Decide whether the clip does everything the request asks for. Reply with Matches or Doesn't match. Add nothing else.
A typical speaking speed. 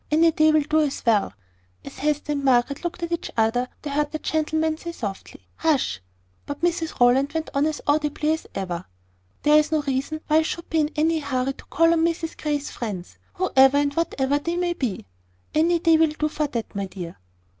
Doesn't match